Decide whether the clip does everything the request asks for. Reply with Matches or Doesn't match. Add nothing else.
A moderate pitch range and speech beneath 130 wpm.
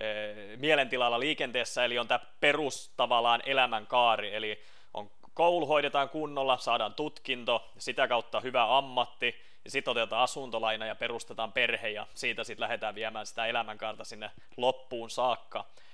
Doesn't match